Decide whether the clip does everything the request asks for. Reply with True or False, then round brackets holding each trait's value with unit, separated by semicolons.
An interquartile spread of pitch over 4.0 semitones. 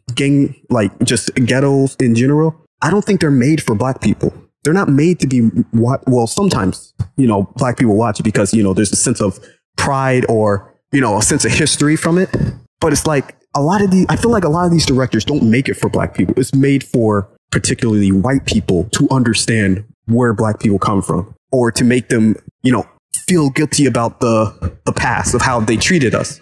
True (4.4 semitones)